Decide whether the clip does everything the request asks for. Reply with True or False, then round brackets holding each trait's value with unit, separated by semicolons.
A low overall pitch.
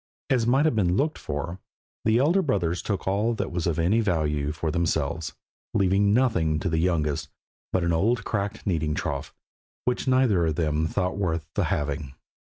True (90 Hz)